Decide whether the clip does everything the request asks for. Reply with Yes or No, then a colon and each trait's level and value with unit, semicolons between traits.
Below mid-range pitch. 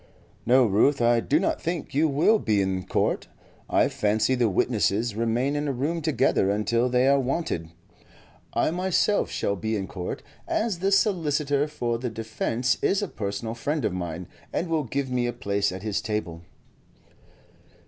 Yes: low, 120 Hz